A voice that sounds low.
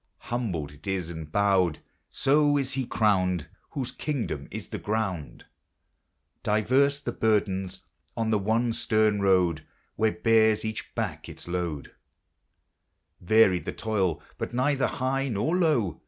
Yes: low, 110 Hz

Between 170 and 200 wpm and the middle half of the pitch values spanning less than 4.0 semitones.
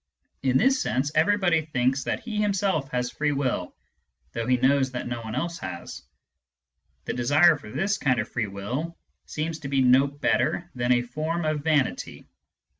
No: average, 180 wpm; average, 4.6 semitones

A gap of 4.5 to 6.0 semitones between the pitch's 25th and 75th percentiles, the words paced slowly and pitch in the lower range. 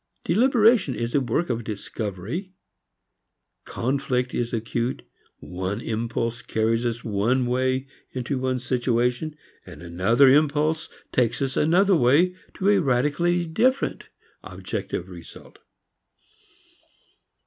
Yes: average, 5.2 semitones; slow, 105 wpm; low, 130 Hz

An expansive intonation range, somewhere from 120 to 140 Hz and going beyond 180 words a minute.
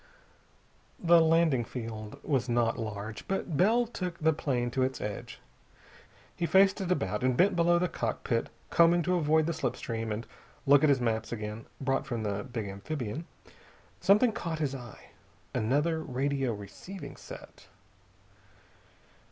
No: wide, 6.7 semitones; low, 135 Hz; average, 150 wpm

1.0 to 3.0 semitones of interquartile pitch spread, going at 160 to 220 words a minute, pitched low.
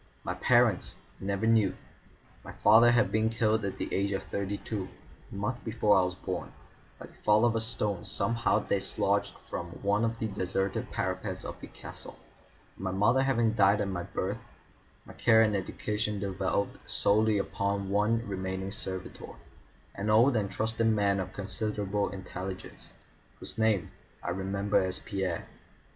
Yes: narrow, 2.4 semitones; average, 165 wpm; low, 100 Hz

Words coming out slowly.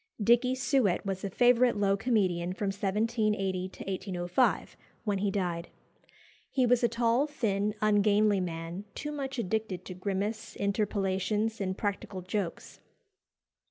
Yes: slow, 130 wpm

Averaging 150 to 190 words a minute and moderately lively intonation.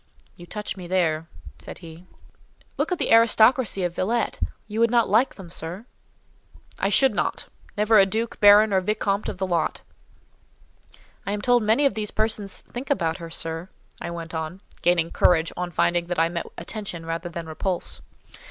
Yes: average, 170 wpm; average, 4.2 semitones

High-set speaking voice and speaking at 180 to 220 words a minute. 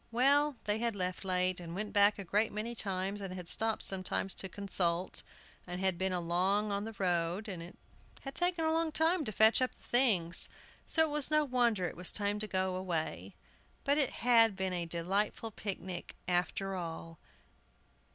Yes: high, 200 Hz; average, 185 wpm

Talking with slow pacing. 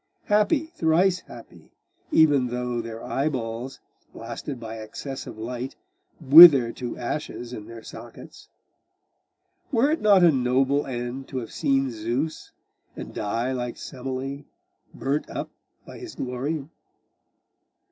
Yes: slow, 125 wpm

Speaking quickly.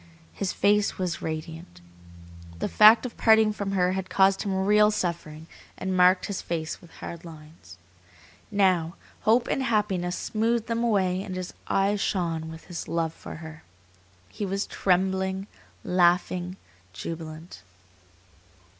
No: slow, 135 wpm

